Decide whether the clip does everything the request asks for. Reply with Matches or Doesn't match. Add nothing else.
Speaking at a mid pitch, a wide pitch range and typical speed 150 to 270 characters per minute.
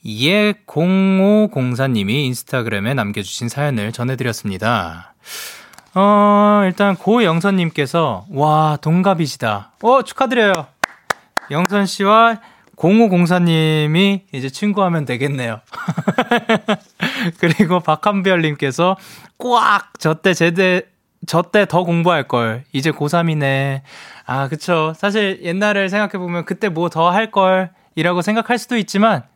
Matches